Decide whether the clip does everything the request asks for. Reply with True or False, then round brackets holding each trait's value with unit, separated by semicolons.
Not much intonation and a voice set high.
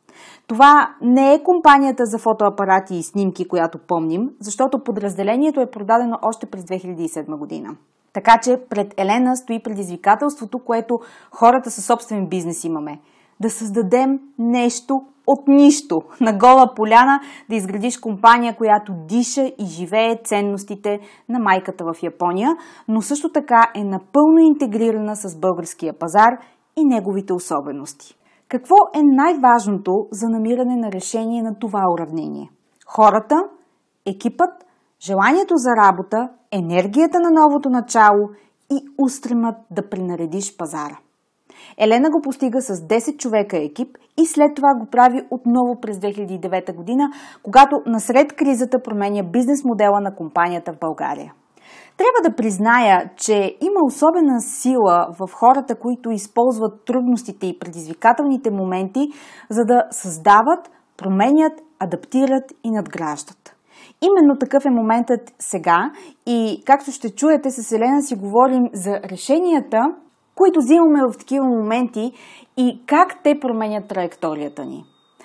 False (5.4 semitones; 230 Hz)